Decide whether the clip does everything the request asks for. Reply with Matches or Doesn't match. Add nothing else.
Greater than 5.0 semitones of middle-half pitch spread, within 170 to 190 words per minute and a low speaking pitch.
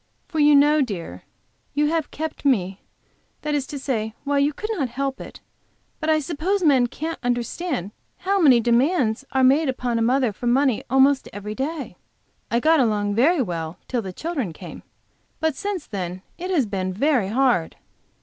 Doesn't match